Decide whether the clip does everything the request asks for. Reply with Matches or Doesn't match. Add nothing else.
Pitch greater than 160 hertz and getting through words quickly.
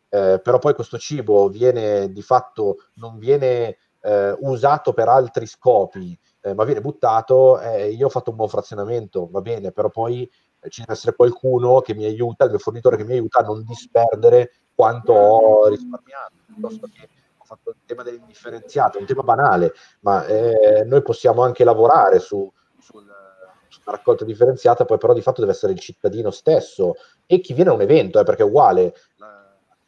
Doesn't match